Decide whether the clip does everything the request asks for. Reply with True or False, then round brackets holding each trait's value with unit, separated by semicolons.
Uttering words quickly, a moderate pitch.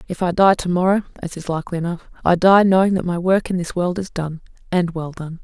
True (255 wpm; 175 Hz)